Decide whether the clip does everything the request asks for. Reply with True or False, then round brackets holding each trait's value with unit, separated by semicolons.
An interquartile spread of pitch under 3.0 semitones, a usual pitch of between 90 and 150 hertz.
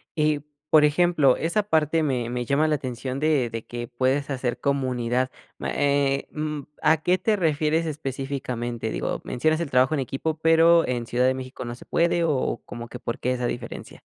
False (3.8 semitones; 140 Hz)